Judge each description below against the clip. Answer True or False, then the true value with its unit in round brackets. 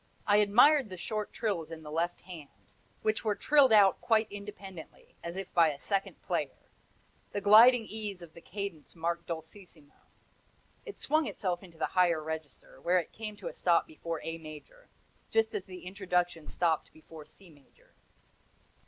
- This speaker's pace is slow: False (170 wpm)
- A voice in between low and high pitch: True (180 Hz)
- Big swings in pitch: False (4.2 semitones)